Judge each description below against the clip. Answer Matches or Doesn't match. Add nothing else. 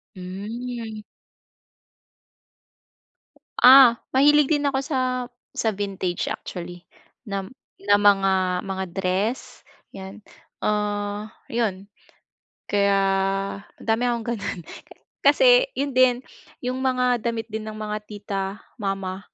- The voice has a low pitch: Doesn't match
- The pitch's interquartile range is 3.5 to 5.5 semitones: Matches